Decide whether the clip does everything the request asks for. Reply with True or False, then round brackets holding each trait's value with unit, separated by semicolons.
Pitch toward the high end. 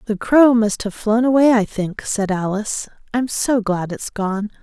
True (220 Hz)